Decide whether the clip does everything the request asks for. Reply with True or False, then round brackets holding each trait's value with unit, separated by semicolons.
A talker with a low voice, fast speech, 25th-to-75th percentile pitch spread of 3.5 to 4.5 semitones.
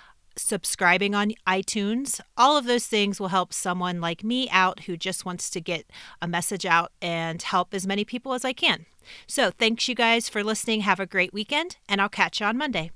False (200 Hz; 210 wpm; 4.0 semitones)